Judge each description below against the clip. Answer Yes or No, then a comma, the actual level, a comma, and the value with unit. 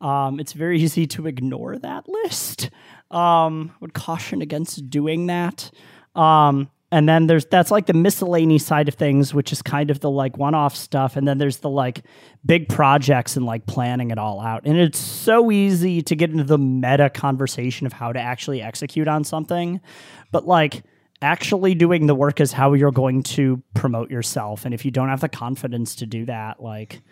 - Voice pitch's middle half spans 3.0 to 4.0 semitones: Yes, average, 3.7 semitones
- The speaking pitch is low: No, medium, 145 Hz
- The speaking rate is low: No, average, 195 wpm